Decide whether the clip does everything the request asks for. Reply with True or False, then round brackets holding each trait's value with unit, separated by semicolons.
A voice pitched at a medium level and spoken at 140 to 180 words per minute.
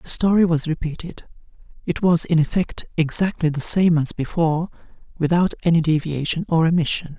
True (165 Hz; 150 wpm)